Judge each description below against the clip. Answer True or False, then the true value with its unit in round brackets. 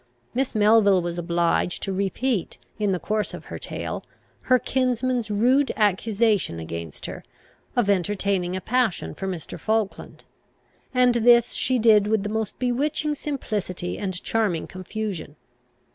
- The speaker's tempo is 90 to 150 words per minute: True (140 wpm)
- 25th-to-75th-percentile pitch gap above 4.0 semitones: True (4.5 semitones)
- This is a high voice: True (210 Hz)